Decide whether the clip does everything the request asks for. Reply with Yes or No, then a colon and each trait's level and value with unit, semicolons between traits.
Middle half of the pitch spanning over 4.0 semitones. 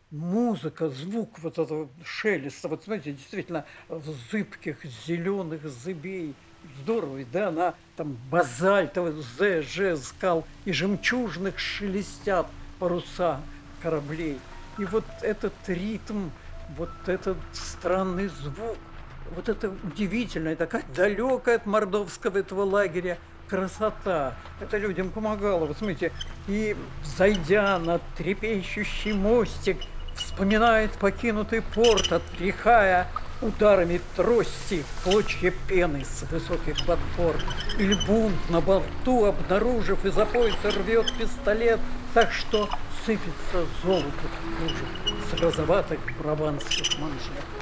Yes: average, 4.4 semitones